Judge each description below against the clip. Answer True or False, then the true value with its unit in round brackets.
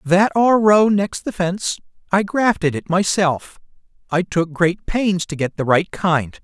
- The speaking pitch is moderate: True (180 Hz)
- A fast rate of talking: False (175 wpm)